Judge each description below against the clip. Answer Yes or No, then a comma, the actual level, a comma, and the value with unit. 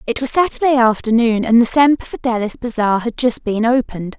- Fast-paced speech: No, average, 185 wpm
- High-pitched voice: Yes, high, 235 Hz